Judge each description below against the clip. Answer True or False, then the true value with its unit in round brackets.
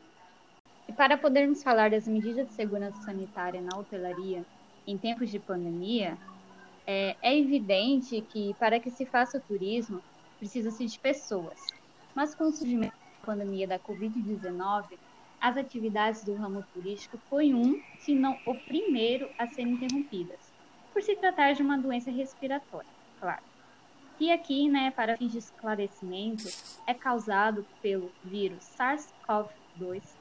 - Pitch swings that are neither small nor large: True (5.0 semitones)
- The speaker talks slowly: False (135 wpm)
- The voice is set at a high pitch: True (225 Hz)